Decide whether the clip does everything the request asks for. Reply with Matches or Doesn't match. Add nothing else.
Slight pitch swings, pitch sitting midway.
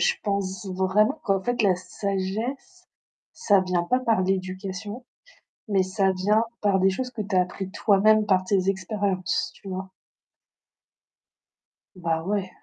Doesn't match